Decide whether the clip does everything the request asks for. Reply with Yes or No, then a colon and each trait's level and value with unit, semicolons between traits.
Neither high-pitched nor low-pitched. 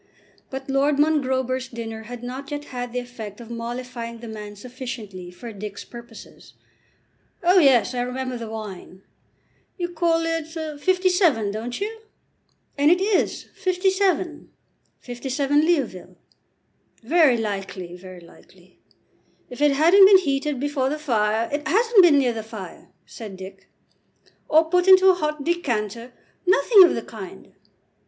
No: very high, 260 Hz